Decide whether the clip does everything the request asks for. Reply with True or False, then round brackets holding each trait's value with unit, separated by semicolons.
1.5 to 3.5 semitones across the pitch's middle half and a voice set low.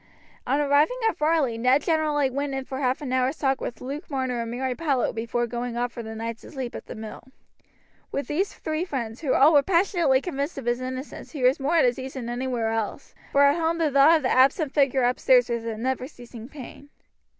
False (3.2 semitones; 265 Hz)